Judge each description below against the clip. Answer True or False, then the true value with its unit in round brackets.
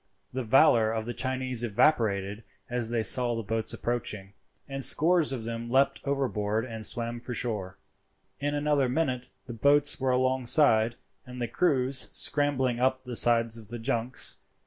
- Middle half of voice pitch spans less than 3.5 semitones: True (2.7 semitones)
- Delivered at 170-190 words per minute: False (160 wpm)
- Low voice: True (120 Hz)